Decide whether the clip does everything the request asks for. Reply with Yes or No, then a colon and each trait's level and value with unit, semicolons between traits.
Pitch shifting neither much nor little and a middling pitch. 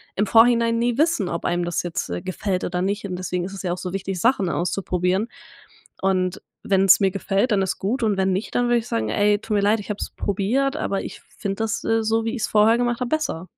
No: average, 3.5 semitones; high, 200 Hz